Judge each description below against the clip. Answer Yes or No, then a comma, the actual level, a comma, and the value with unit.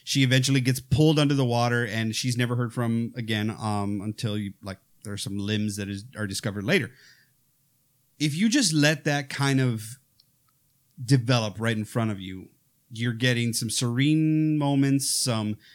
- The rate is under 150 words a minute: No, average, 170 wpm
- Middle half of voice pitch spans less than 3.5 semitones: No, average, 3.9 semitones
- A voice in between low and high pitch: No, low, 125 Hz